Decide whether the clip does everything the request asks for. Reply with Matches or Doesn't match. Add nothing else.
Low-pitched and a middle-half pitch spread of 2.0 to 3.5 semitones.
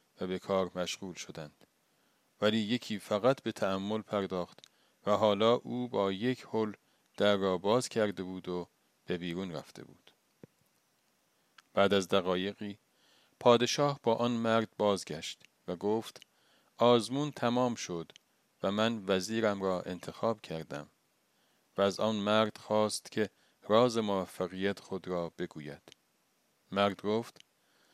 Matches